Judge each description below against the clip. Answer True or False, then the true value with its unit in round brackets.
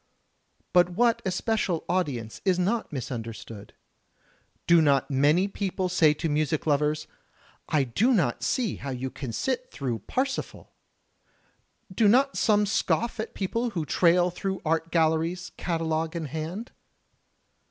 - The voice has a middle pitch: True (170 Hz)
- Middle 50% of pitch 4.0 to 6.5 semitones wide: True (5.2 semitones)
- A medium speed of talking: False (130 wpm)